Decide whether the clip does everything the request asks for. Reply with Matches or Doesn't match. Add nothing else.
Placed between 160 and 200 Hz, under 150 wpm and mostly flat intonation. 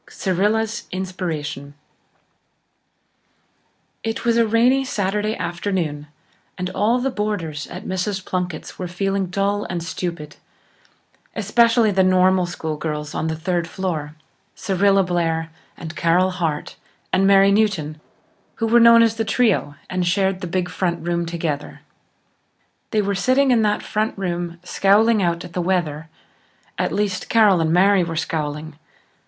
Doesn't match